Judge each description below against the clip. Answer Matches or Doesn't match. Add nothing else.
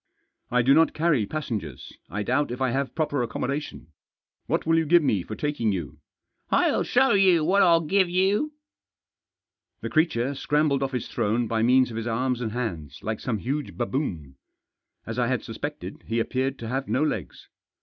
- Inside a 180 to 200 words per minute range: Matches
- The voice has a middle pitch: Doesn't match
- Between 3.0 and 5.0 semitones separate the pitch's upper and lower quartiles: Doesn't match